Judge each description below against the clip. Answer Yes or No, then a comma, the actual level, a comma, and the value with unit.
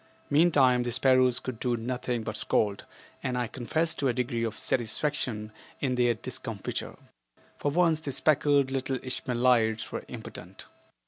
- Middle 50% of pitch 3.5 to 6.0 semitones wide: No, average, 2.7 semitones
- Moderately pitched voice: No, low, 125 Hz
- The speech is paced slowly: No, average, 145 wpm